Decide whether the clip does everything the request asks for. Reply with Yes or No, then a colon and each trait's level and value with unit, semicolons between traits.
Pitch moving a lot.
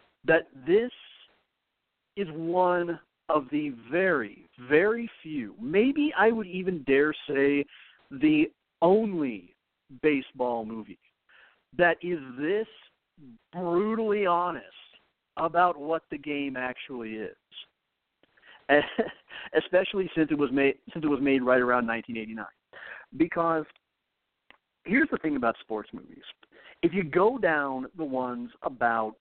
Yes: wide, 6.0 semitones